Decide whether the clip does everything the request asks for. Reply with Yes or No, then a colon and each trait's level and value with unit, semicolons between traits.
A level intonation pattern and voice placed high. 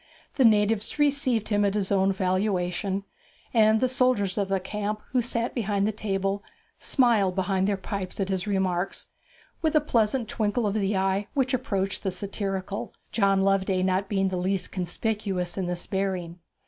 Yes: narrow, 2.2 semitones; high, 200 Hz